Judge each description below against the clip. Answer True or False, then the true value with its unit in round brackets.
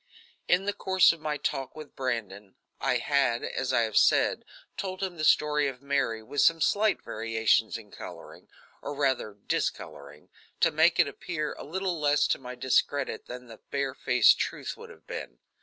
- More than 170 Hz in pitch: False (140 Hz)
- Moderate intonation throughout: True (4.9 semitones)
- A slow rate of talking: False (175 wpm)